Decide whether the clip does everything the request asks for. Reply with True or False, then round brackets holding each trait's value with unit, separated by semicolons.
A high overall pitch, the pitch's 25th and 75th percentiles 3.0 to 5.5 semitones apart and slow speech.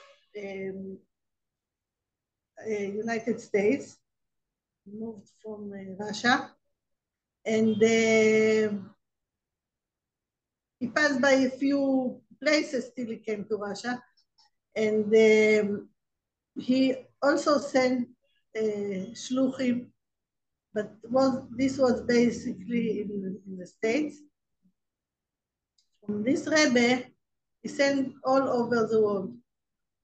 True (230 Hz; 3.8 semitones; 95 wpm)